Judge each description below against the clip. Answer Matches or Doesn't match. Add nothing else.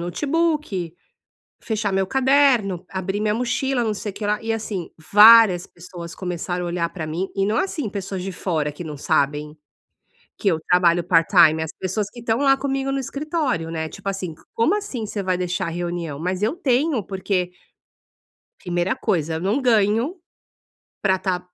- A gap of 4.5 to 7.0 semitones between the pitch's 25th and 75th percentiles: Matches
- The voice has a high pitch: Matches